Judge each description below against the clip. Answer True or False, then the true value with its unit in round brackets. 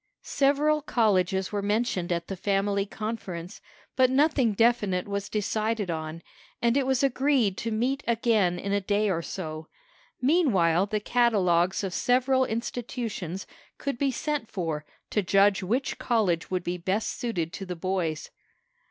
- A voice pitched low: False (205 Hz)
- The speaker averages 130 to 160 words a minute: True (150 wpm)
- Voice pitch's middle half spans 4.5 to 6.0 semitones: True (4.9 semitones)